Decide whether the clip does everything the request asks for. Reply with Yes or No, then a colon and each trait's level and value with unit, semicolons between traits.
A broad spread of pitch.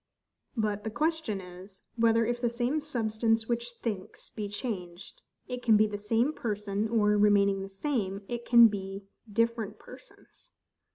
No: average, 2.7 semitones